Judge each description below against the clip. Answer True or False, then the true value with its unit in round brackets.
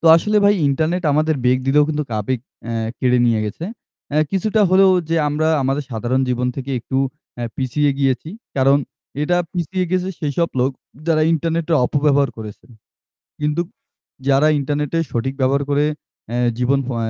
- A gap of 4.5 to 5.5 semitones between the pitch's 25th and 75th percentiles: False (3.6 semitones)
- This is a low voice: False (145 Hz)